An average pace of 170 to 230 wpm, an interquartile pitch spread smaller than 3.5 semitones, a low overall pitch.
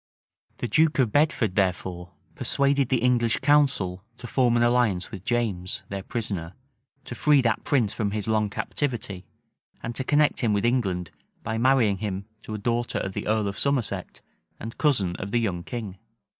No: average, 175 wpm; average, 4.2 semitones; low, 110 Hz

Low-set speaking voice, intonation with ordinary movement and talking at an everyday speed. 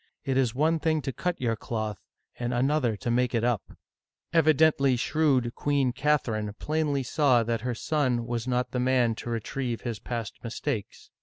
Yes: low, 125 Hz; average, 3.6 semitones; average, 175 wpm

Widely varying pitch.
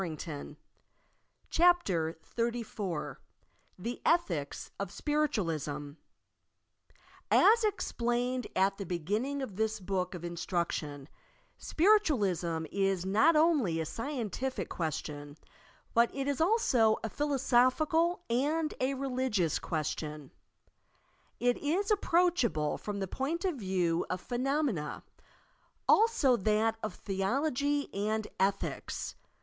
Yes: wide, 8.1 semitones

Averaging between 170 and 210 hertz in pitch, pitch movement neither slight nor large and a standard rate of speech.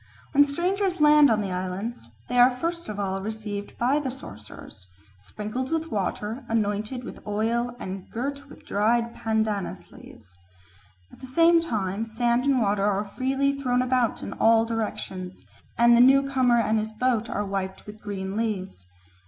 No: high, 225 Hz; average, 4.2 semitones; average, 160 wpm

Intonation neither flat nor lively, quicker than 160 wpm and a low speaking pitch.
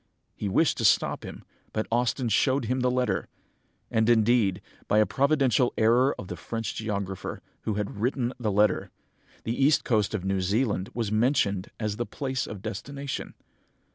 Yes: average, 3.5 semitones; average, 170 wpm; low, 115 Hz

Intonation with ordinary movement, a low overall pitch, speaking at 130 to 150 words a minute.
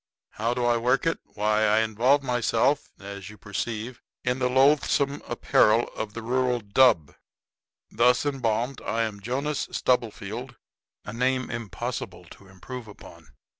Yes: average, 3.1 semitones; low, 120 Hz; average, 140 wpm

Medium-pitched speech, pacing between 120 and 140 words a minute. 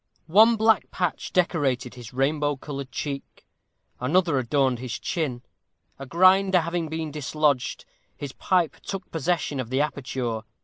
Yes: medium, 150 Hz; slow, 135 wpm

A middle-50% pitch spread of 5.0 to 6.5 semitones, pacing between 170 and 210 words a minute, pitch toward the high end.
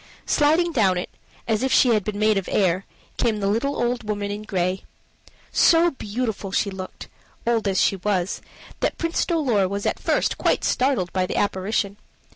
No: average, 4.0 semitones; average, 180 wpm; high, 210 Hz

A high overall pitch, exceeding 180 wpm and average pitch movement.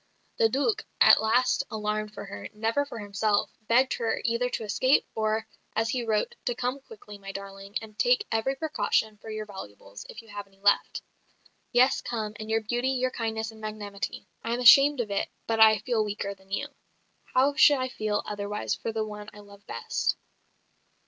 Yes: high, 220 Hz; average, 190 wpm; average, 3.0 semitones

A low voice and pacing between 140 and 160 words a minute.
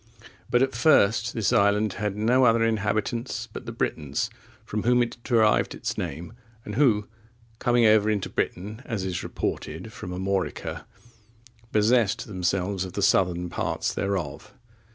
Yes: low, 105 Hz; average, 145 wpm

